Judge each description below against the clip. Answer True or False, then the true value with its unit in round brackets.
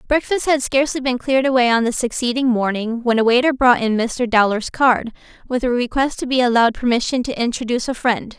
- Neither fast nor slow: False (210 wpm)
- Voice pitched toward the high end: True (245 Hz)